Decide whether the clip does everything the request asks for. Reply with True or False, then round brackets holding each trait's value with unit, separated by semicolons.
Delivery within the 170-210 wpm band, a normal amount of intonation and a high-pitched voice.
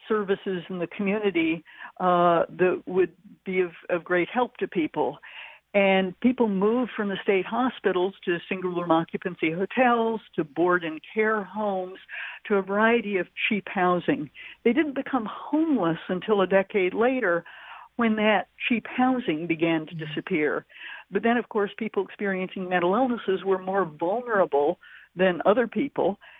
False (150 wpm; 3.8 semitones; 195 Hz)